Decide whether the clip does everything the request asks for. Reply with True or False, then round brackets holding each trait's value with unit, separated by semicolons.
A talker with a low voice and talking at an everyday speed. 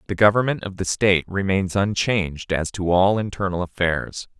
True (95 Hz; 165 wpm)